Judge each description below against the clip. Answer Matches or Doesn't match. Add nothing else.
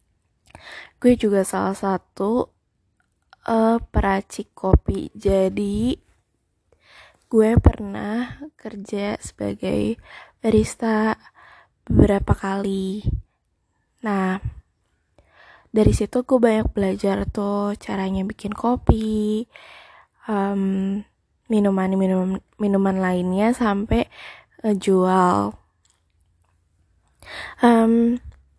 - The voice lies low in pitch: Doesn't match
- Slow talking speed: Matches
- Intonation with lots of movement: Doesn't match